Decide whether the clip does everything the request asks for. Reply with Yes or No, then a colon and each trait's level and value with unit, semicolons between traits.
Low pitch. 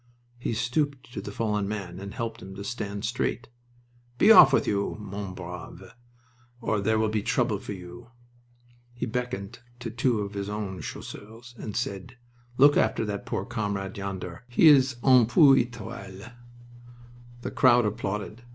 Yes: low, 110 Hz